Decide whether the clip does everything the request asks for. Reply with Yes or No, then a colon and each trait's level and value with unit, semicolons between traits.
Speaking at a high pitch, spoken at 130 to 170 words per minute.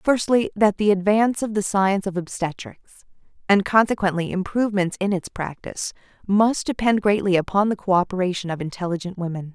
Yes: high, 195 Hz; average, 150 wpm